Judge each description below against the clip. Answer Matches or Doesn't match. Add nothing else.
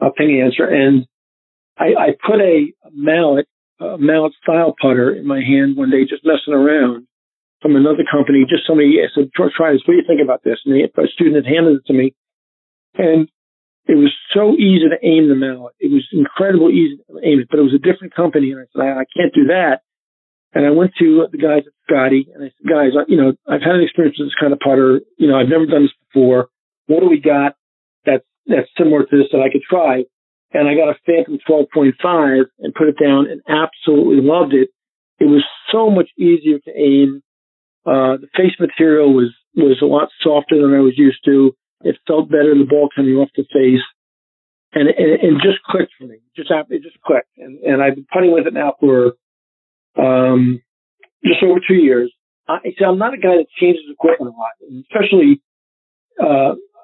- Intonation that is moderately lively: Matches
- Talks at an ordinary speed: Doesn't match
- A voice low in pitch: Doesn't match